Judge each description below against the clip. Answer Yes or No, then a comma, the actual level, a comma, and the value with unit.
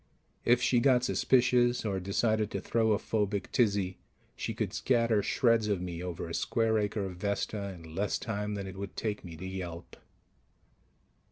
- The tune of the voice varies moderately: Yes, average, 3.4 semitones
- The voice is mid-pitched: No, low, 105 Hz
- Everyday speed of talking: Yes, average, 175 wpm